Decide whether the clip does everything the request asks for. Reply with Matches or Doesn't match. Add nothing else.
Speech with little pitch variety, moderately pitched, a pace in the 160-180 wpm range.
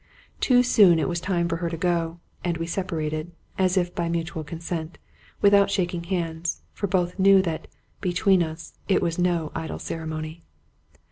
Matches